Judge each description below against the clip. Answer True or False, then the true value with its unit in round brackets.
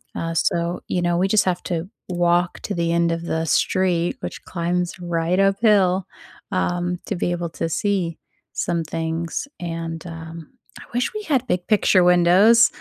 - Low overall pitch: False (175 Hz)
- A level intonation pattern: True (1.8 semitones)